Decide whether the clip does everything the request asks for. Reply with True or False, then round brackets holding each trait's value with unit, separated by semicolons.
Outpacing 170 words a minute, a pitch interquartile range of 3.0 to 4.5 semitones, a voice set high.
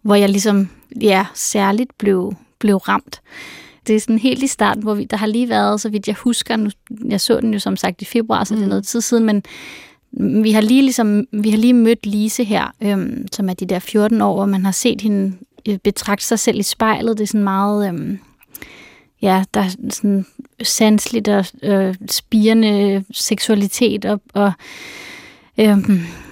False (190 wpm; 2.4 semitones; 215 Hz)